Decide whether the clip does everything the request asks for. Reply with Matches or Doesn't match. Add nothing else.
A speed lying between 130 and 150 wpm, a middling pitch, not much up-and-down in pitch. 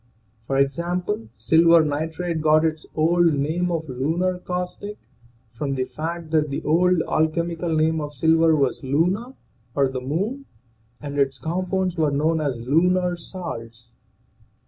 Doesn't match